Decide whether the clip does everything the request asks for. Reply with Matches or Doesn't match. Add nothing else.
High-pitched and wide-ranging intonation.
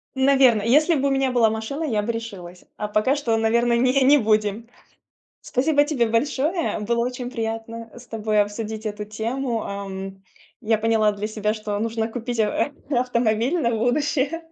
Doesn't match